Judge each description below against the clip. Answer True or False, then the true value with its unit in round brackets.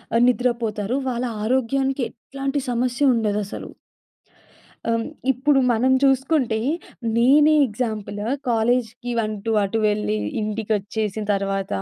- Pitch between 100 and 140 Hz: False (230 Hz)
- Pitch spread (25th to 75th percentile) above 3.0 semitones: True (3.5 semitones)